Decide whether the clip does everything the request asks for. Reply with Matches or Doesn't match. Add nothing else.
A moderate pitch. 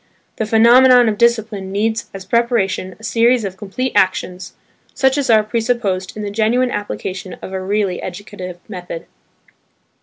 Doesn't match